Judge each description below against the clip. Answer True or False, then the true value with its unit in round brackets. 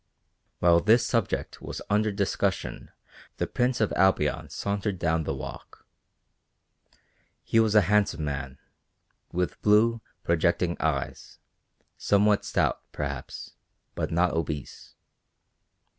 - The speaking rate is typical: False (110 wpm)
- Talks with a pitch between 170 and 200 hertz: False (95 Hz)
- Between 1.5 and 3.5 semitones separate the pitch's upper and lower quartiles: False (4.6 semitones)